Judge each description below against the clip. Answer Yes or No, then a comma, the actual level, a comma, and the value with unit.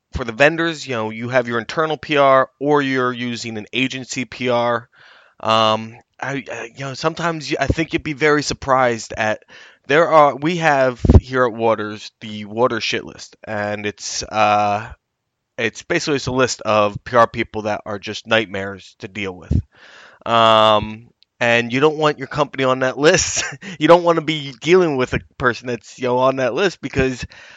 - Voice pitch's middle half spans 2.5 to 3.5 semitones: No, average, 4.5 semitones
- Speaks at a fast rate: No, average, 185 wpm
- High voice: No, low, 125 Hz